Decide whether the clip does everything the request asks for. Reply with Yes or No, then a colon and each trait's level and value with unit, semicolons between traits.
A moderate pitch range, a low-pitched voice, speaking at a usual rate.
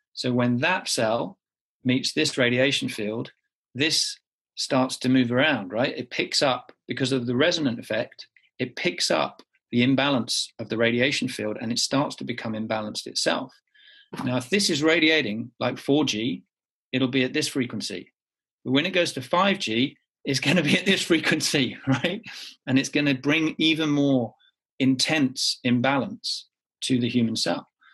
Yes: average, 3.9 semitones; low, 130 Hz; average, 165 wpm